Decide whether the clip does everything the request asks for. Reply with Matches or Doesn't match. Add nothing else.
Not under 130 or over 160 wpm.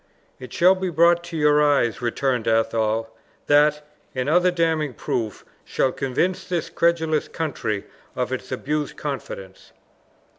Matches